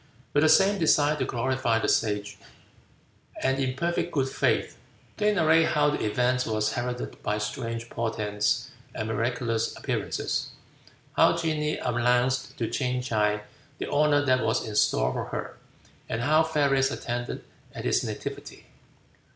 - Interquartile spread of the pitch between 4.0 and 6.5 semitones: Yes, average, 4.4 semitones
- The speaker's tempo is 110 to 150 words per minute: Yes, average, 145 wpm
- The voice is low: Yes, low, 125 Hz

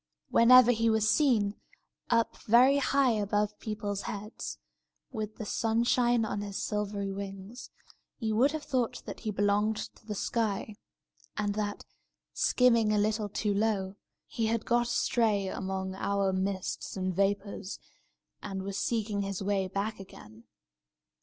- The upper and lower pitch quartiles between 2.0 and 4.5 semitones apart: Yes, narrow, 2.4 semitones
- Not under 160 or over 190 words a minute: No, average, 140 wpm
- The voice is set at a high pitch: Yes, high, 210 Hz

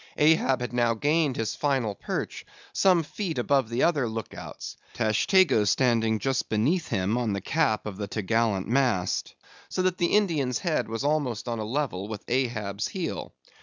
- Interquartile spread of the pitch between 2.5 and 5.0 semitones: No, wide, 5.5 semitones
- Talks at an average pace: Yes, average, 175 wpm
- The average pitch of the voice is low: Yes, low, 120 Hz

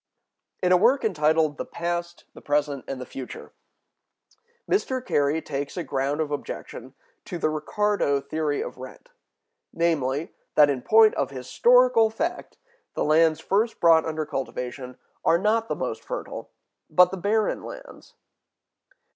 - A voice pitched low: No, medium, 160 Hz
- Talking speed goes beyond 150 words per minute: No, average, 145 wpm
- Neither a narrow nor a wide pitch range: No, wide, 6.5 semitones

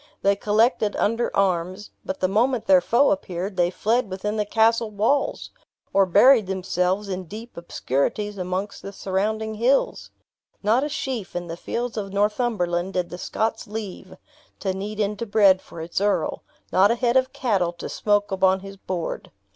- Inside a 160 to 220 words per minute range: Yes, average, 170 wpm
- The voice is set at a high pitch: Yes, high, 205 Hz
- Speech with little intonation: No, average, 3.0 semitones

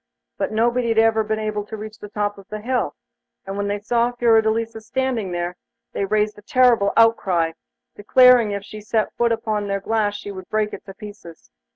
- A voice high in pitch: Yes, high, 215 Hz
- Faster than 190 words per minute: Yes, fast, 205 wpm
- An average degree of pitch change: No, narrow, 2.0 semitones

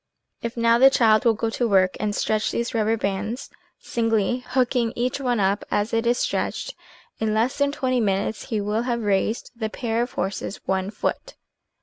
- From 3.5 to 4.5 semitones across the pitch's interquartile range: No, narrow, 2.4 semitones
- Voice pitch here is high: Yes, high, 225 Hz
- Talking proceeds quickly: No, average, 190 wpm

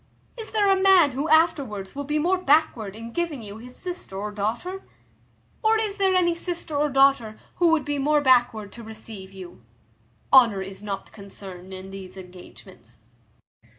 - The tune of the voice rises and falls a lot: Yes, wide, 8.9 semitones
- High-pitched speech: Yes, very high, 250 Hz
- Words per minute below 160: No, average, 170 wpm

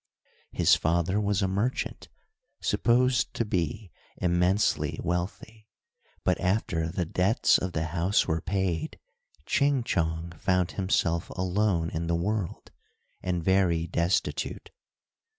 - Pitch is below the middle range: Yes, very low, 90 Hz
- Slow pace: Yes, slow, 115 wpm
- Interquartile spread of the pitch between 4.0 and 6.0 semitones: No, average, 3.4 semitones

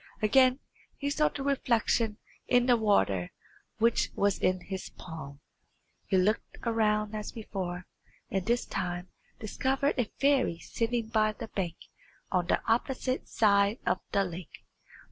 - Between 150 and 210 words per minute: No, average, 140 wpm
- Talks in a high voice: Yes, high, 215 Hz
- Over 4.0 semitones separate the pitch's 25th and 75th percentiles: Yes, average, 4.6 semitones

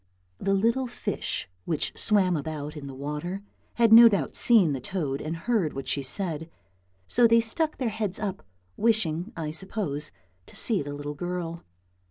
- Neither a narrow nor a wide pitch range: No, wide, 6.7 semitones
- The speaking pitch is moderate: Yes, medium, 180 Hz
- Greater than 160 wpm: Yes, average, 170 wpm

